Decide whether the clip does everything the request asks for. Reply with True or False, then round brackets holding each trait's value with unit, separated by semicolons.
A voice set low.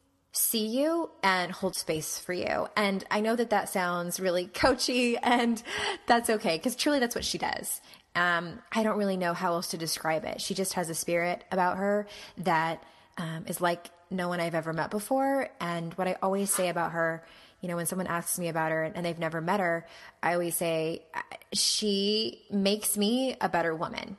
False (180 Hz)